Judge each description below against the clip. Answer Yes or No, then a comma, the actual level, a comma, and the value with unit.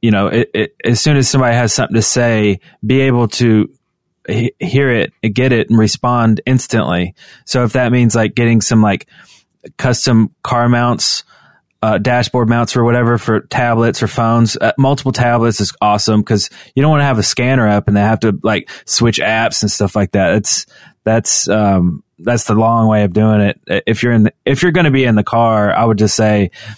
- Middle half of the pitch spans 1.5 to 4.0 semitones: Yes, narrow, 2.4 semitones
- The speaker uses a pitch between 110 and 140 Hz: Yes, low, 115 Hz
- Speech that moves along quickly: Yes, fast, 210 wpm